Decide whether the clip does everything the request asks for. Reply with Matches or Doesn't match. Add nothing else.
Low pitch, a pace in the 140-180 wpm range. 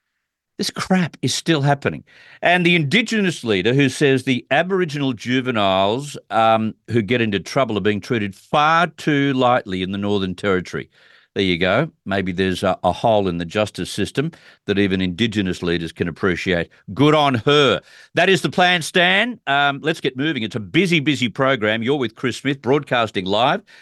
Matches